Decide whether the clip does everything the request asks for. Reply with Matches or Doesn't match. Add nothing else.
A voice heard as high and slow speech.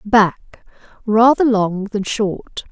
Matches